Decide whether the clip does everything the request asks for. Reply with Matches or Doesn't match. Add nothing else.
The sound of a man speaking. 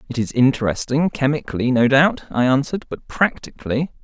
Matches